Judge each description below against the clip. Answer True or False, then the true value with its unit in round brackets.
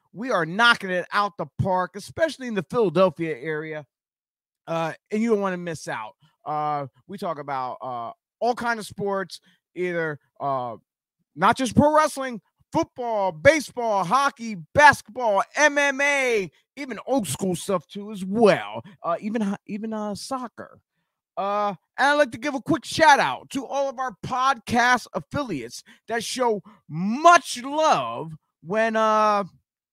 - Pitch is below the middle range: False (210 Hz)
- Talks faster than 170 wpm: False (150 wpm)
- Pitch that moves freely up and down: True (6.9 semitones)